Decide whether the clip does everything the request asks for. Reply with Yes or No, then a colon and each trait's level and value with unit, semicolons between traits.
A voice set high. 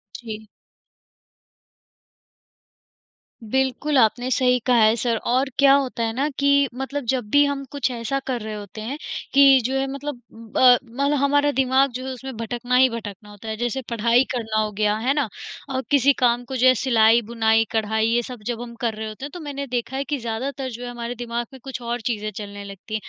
Yes: high, 245 Hz